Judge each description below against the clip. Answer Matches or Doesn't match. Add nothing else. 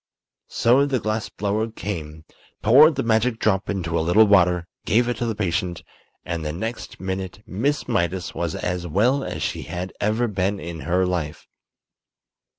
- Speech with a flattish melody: Doesn't match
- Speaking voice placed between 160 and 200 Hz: Doesn't match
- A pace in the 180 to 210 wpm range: Doesn't match